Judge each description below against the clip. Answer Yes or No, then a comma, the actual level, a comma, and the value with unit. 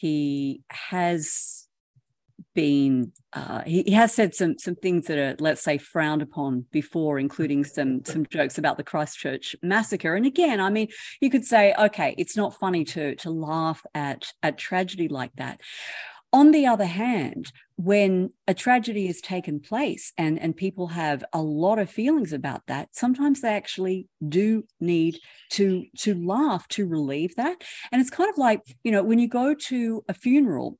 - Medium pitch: Yes, medium, 180 Hz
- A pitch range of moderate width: No, wide, 6.6 semitones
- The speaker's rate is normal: Yes, average, 175 wpm